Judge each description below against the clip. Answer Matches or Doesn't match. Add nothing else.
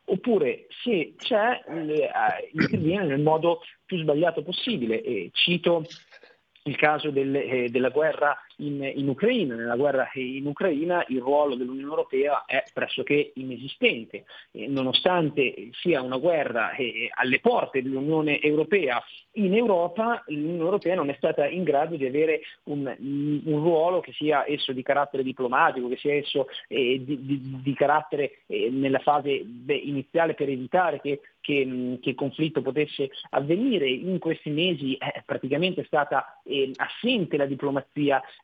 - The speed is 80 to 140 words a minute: Doesn't match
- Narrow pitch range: Doesn't match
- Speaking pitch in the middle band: Matches